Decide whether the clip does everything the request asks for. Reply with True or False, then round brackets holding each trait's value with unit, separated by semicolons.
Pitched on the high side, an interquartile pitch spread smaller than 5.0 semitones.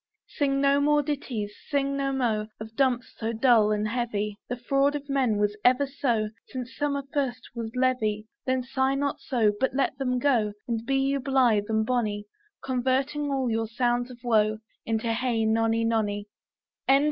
True (245 Hz; 3.5 semitones)